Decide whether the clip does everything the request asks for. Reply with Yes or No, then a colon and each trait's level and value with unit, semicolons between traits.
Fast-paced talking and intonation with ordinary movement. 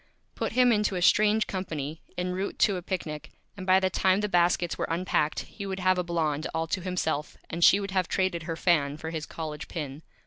Yes: fast, 220 wpm; average, 3.0 semitones